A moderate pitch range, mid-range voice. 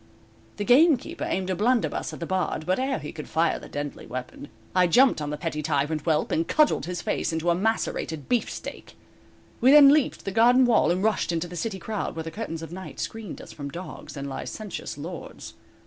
No: wide, 6.0 semitones; medium, 180 Hz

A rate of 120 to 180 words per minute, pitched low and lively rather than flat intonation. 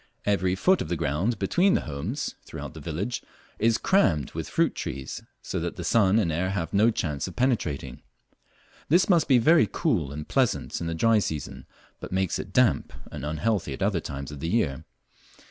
No: average, 190 wpm; very low, 95 Hz; wide, 6.8 semitones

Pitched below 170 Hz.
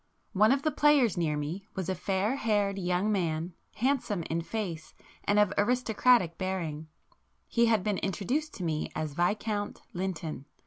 No: high, 195 Hz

